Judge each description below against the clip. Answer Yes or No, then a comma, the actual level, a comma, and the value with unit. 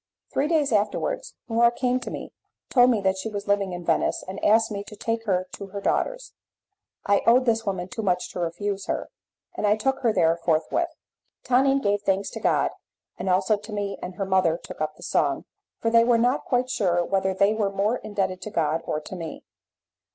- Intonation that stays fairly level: No, average, 3.6 semitones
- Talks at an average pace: No, fast, 210 wpm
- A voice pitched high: Yes, high, 205 Hz